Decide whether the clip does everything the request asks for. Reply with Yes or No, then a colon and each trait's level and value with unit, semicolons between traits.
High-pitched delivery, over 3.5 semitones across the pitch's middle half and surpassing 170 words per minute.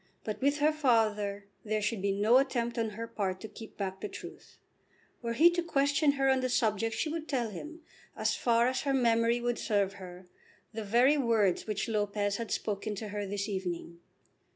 Yes: high, 225 Hz; average, 4.1 semitones; average, 200 wpm